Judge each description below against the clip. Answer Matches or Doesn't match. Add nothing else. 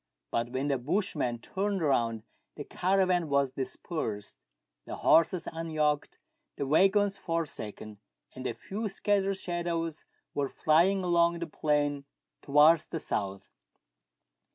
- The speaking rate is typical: Doesn't match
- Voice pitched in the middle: Matches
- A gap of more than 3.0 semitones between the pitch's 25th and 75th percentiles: Matches